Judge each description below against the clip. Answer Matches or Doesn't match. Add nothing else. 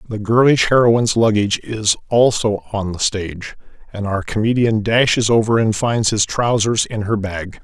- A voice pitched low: Matches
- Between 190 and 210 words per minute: Doesn't match